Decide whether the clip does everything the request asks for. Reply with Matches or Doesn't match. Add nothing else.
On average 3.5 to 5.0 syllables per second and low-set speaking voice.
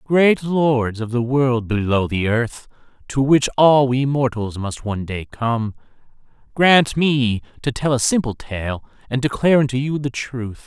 Matches